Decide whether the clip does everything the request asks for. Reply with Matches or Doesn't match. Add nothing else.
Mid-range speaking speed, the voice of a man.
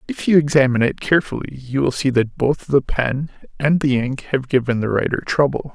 Doesn't match